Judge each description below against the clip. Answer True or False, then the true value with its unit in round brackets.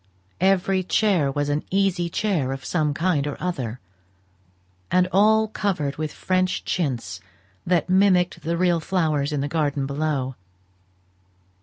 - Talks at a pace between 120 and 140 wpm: True (135 wpm)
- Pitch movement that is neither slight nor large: True (4.3 semitones)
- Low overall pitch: False (170 Hz)